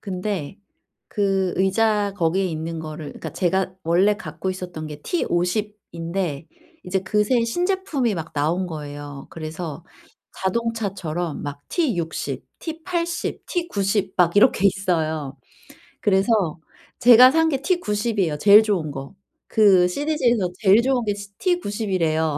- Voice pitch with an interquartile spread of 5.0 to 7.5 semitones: Yes, average, 5.3 semitones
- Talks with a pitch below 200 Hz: Yes, high, 190 Hz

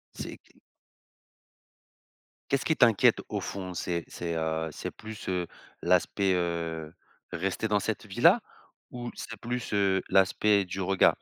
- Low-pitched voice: Yes, very low, 95 Hz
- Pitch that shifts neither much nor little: Yes, average, 3.8 semitones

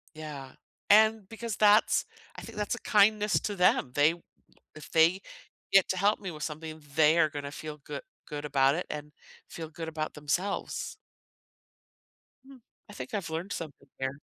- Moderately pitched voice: Yes, medium, 160 Hz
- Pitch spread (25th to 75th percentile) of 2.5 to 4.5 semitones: No, average, 5.3 semitones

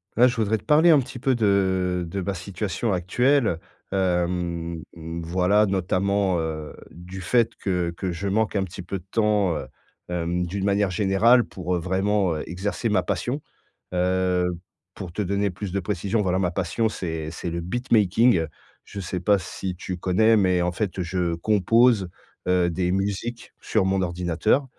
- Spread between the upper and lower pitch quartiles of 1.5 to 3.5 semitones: Yes, average, 2.8 semitones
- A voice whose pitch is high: No, very low, 95 Hz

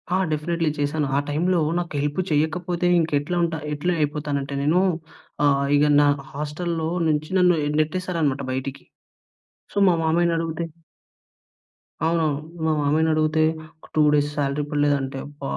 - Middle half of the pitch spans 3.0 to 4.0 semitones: No, narrow, 2.5 semitones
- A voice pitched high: No, medium, 155 Hz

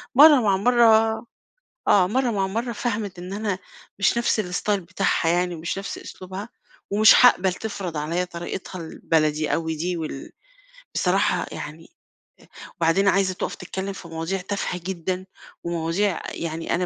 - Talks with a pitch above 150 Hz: Yes, medium, 185 Hz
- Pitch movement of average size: Yes, average, 3.3 semitones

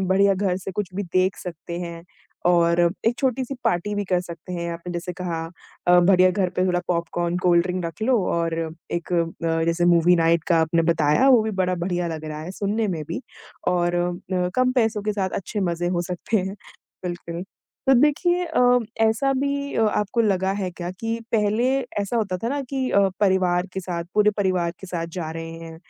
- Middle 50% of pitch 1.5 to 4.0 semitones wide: Yes, average, 3.5 semitones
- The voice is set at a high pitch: No, medium, 180 Hz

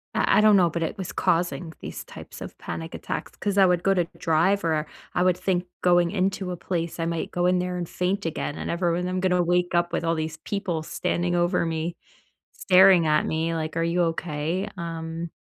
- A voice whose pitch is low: No, medium, 175 Hz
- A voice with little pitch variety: Yes, narrow, 1.7 semitones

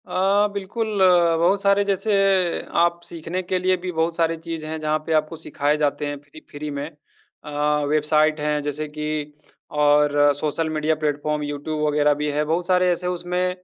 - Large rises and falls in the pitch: No, average, 3.2 semitones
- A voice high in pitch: No, medium, 155 Hz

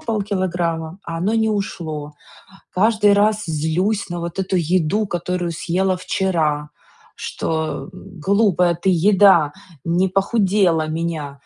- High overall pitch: No, medium, 180 Hz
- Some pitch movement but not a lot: Yes, average, 3.4 semitones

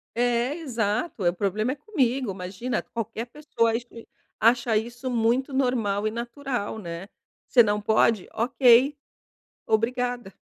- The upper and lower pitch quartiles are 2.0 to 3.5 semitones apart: Yes, average, 2.7 semitones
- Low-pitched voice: No, high, 235 Hz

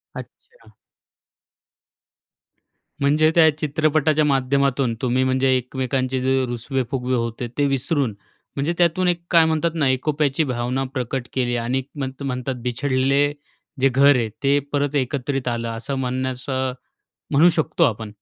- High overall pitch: No, low, 135 Hz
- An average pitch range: No, narrow, 2.2 semitones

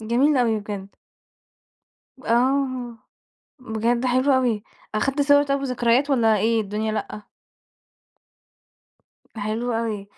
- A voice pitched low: No, high, 235 Hz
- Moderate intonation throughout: Yes, average, 3.1 semitones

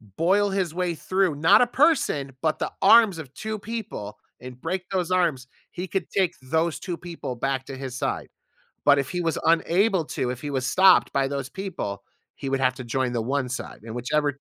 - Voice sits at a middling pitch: Yes, medium, 160 Hz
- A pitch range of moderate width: No, wide, 6.0 semitones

